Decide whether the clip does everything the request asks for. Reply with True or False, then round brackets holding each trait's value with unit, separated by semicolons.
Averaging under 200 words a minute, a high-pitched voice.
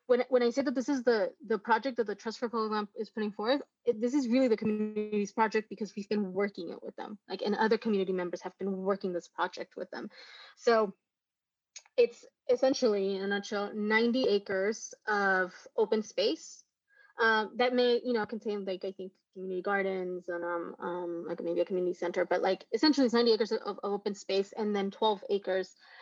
False (205 wpm; 215 Hz)